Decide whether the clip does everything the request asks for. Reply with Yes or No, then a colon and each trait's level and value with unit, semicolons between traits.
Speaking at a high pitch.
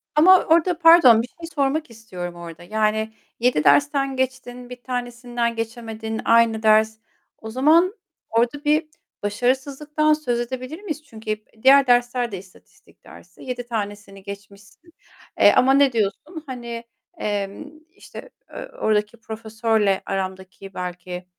Yes: high, 235 Hz